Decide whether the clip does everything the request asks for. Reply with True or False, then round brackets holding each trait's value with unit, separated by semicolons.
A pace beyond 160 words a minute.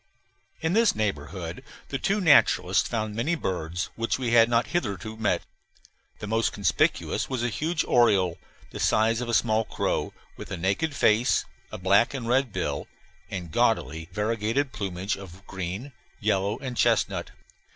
False (155 wpm)